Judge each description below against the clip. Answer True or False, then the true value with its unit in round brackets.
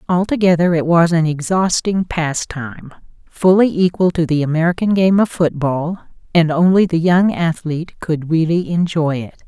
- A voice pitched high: False (170 Hz)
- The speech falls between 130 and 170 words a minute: True (140 wpm)